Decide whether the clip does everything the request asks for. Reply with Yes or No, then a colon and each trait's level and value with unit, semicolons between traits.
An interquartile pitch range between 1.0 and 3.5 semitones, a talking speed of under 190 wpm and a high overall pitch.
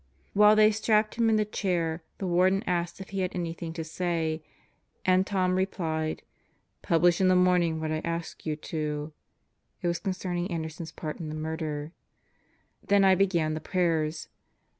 No: average, 2.9 semitones; average, 170 wpm; medium, 175 Hz